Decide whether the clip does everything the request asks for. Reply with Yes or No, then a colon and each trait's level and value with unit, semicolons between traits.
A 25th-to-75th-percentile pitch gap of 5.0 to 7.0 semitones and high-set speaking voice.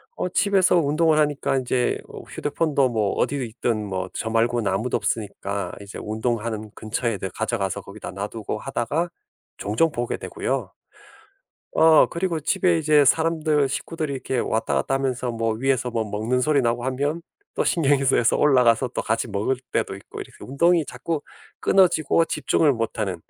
No: average, 5.3 semitones; low, 125 Hz